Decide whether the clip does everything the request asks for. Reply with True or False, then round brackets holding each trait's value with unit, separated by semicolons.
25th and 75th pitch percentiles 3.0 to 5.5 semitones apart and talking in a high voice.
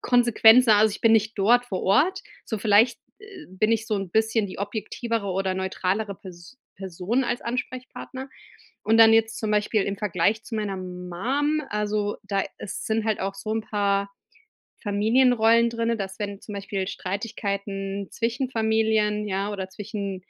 False (2.5 semitones; 210 Hz)